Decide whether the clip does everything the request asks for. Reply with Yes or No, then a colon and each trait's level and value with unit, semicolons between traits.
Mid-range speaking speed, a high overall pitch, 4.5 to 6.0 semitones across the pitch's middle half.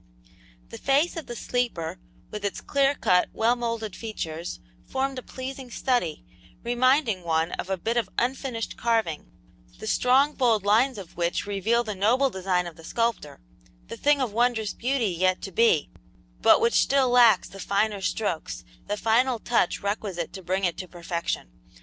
Yes: average, 170 wpm; high, 220 Hz; average, 5.0 semitones